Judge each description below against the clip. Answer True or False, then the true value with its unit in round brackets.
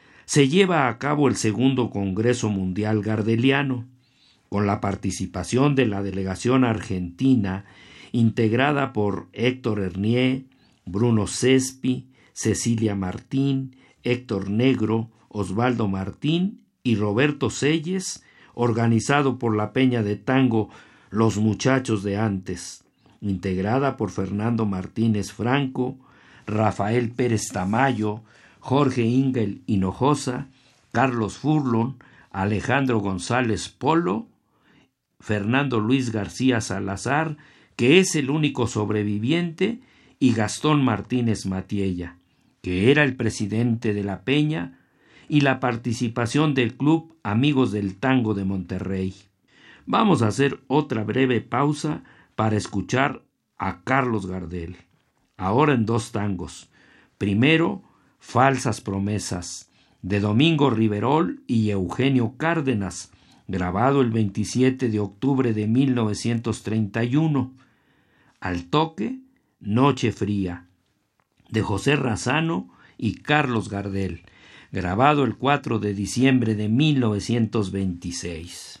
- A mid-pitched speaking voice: False (115 Hz)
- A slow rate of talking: True (105 wpm)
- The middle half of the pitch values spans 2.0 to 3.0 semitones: False (4.7 semitones)